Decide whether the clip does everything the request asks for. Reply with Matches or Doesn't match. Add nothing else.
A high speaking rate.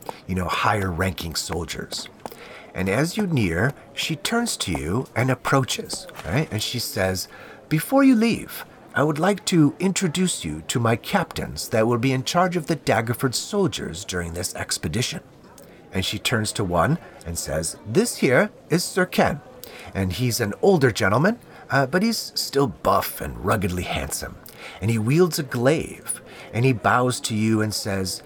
Doesn't match